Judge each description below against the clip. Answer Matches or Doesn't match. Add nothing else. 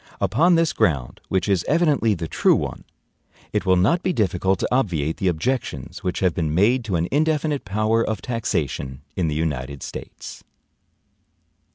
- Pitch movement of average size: Doesn't match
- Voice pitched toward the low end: Matches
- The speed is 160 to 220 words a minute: Matches